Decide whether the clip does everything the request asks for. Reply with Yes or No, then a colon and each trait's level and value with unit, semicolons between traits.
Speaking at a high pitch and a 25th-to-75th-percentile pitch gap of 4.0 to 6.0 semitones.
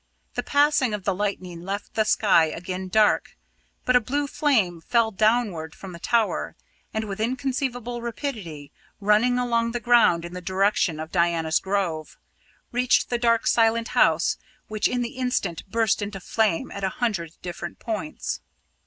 Yes: high, 215 Hz; average, 4.8 semitones